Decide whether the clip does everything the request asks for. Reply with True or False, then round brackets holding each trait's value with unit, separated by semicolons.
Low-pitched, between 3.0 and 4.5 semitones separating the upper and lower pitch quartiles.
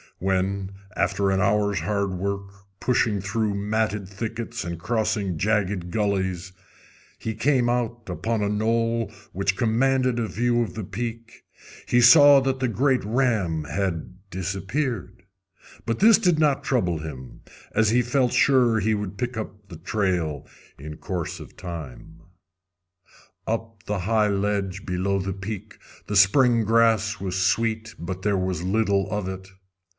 True (105 Hz; 3.5 semitones)